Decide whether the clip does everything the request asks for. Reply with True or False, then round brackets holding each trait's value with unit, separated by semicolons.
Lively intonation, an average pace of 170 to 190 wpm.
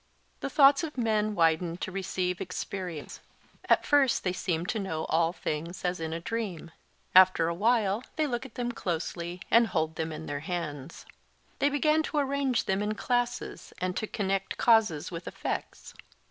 True (5.8 semitones; 175 wpm)